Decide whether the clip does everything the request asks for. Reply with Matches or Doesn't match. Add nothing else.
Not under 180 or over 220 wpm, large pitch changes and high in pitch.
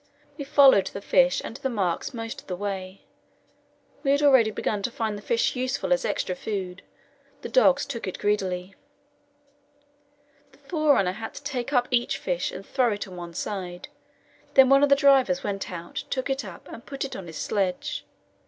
Matches